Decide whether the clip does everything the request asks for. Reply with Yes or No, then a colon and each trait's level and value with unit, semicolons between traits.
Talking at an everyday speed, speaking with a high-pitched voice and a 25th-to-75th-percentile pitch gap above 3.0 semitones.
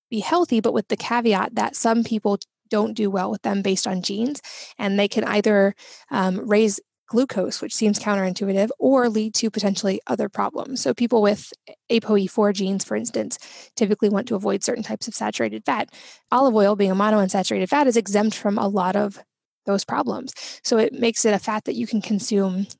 No: average, 190 wpm; high, 210 Hz; narrow, 2.5 semitones